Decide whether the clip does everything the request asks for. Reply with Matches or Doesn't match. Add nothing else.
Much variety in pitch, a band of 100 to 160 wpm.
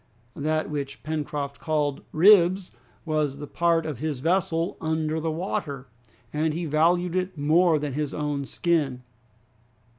Doesn't match